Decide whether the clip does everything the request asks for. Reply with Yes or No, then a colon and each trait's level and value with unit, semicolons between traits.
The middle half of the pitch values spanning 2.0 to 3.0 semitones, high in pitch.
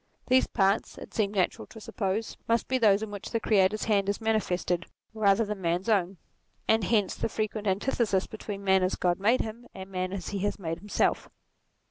Yes: narrow, 2.5 semitones; high, 200 Hz